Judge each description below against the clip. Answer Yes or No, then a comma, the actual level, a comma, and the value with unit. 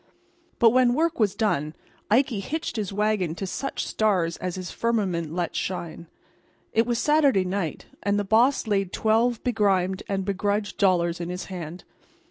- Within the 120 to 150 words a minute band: No, average, 160 wpm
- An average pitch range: Yes, average, 3.9 semitones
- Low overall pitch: No, high, 200 Hz